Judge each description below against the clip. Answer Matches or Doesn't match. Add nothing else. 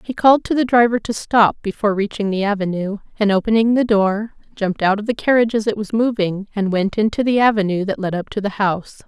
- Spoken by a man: Doesn't match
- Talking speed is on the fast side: Matches